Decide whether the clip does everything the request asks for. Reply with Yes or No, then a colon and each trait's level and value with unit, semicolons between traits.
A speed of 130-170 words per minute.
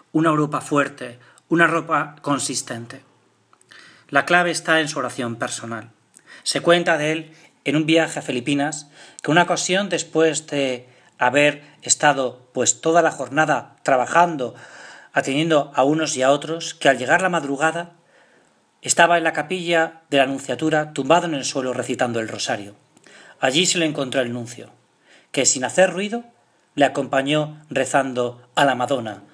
Yes: average, 155 wpm